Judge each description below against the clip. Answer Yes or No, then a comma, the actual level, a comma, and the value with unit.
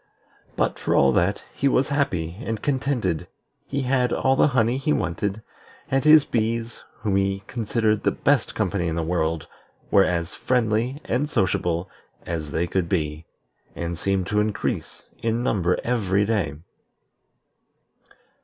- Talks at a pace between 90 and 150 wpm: Yes, average, 145 wpm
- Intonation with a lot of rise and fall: Yes, wide, 6.1 semitones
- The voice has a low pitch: Yes, low, 105 Hz